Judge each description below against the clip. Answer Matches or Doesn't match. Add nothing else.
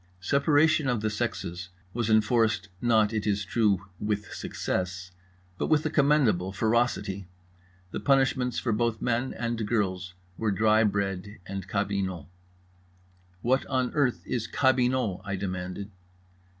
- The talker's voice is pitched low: Matches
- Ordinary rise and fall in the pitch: Matches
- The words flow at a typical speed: Doesn't match